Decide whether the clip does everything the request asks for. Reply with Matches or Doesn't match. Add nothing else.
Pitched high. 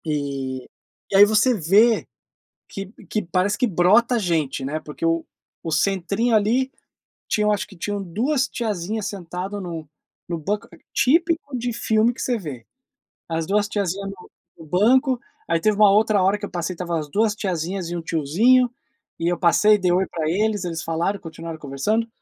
Matches